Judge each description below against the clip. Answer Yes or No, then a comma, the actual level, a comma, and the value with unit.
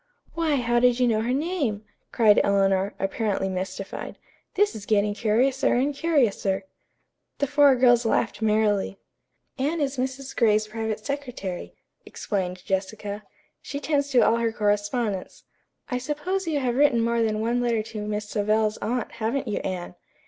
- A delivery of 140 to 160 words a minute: Yes, average, 155 wpm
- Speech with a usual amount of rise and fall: Yes, average, 4.3 semitones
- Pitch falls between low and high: No, high, 230 Hz